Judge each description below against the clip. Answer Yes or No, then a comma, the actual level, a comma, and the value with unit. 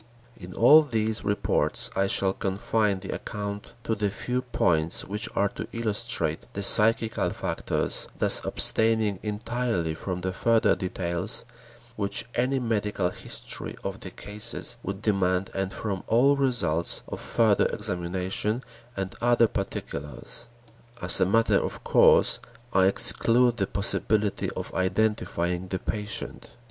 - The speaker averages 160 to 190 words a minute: No, slow, 135 wpm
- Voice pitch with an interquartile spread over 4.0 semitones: No, average, 3.3 semitones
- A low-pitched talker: Yes, low, 105 Hz